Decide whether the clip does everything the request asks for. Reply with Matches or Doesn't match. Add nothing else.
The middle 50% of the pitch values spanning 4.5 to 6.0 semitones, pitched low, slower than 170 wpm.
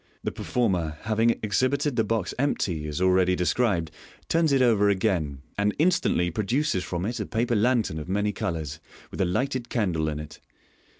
Doesn't match